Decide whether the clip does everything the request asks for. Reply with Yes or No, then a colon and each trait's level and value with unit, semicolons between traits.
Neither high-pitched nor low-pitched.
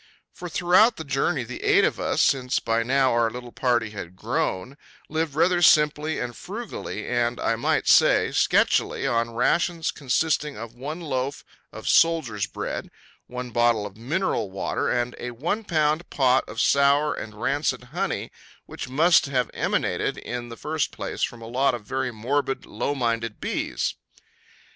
No: low, 130 Hz